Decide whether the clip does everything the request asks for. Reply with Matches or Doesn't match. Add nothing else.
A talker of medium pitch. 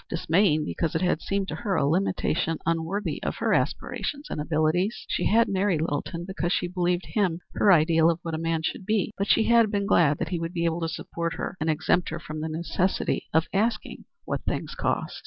Matches